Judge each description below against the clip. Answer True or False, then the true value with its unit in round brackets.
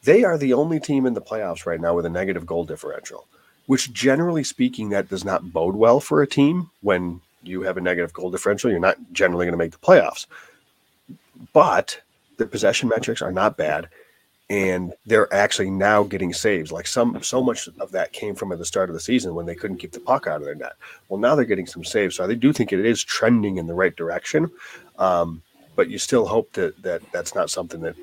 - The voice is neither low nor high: False (100 Hz)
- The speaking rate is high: True (225 wpm)